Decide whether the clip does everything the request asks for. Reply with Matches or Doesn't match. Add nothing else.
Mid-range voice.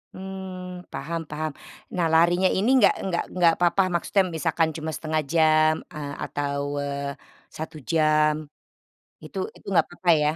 Matches